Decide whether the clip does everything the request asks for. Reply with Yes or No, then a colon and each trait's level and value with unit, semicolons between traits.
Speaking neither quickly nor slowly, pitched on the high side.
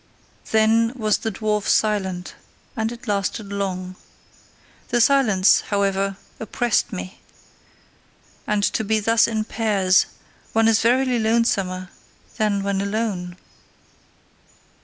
No: slow, 110 wpm; high, 210 Hz